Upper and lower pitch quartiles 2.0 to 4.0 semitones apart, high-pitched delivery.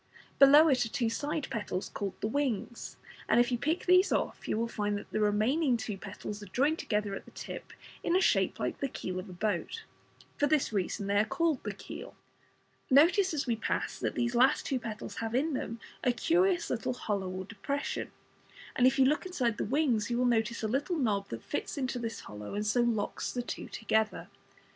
No: average, 5.2 semitones; high, 235 Hz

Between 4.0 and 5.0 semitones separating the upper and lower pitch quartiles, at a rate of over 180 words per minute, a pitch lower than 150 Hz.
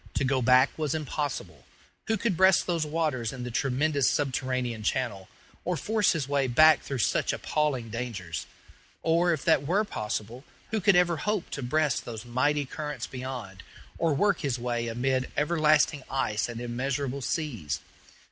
No: average, 4.3 semitones; average, 160 wpm; low, 135 Hz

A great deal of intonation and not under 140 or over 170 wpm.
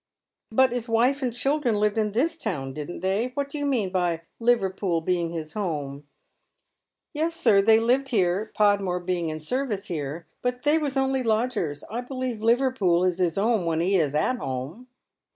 No: wide, 6.3 semitones; average, 190 wpm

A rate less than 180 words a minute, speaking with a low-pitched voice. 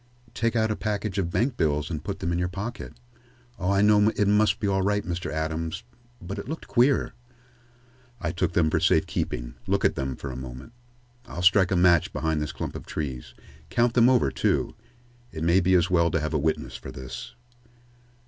No: fast, 205 wpm; very low, 90 Hz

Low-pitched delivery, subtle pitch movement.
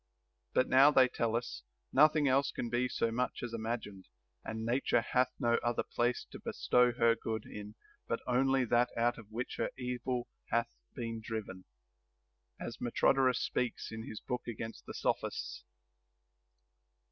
Yes: low, 120 Hz; narrow, 1.9 semitones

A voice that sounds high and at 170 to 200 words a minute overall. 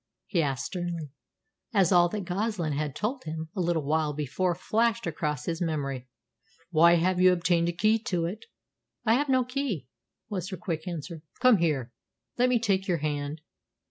No: medium, 175 Hz; average, 185 wpm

